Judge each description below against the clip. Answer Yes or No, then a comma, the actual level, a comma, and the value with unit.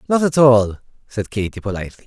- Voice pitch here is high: No, low, 115 Hz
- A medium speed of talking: Yes, average, 175 wpm